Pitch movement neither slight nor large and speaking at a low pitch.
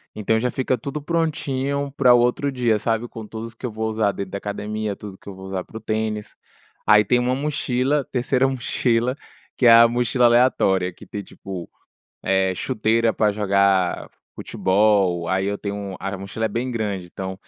Yes: average, 3.9 semitones; low, 110 Hz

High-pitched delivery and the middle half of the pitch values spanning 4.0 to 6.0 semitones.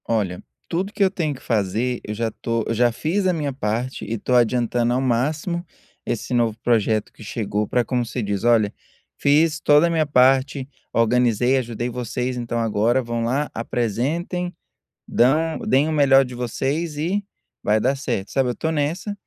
No: low, 125 Hz; average, 4.3 semitones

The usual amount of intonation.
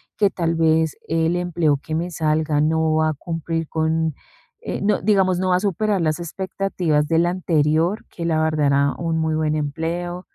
No: narrow, 2.1 semitones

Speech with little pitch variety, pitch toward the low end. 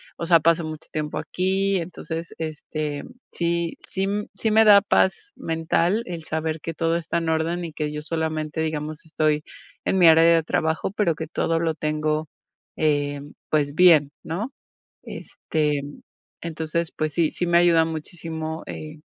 No: narrow, 1.7 semitones; medium, 160 Hz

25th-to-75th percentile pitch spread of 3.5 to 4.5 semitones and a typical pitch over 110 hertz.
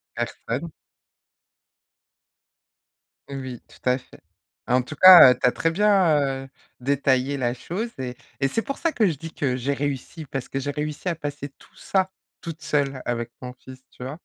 Yes: average, 4.2 semitones; medium, 140 Hz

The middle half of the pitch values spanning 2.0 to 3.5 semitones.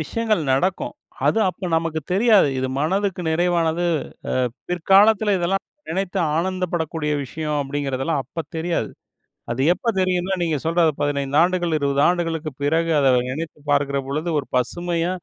No: average, 3.9 semitones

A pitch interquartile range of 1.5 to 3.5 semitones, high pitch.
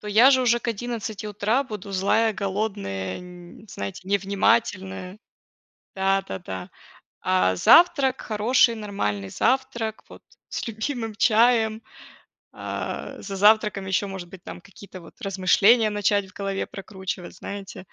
Yes: average, 2.9 semitones; high, 205 Hz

